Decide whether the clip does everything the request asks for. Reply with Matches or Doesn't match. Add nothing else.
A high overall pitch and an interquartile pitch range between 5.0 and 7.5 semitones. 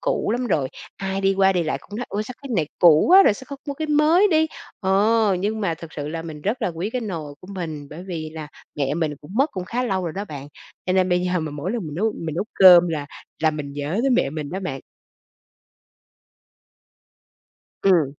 Doesn't match